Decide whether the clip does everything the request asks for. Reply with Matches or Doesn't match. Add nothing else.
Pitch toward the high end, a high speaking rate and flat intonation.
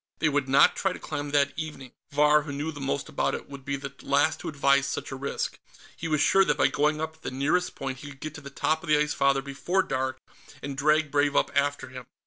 Doesn't match